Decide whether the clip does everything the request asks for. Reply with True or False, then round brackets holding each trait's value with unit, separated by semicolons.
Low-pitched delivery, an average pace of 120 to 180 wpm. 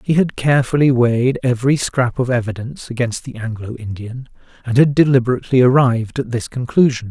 True (125 Hz; 160 wpm)